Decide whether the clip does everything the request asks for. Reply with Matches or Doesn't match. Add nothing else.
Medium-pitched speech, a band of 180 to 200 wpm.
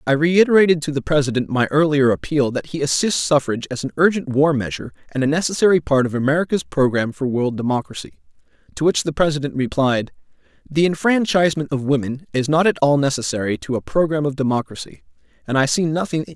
Matches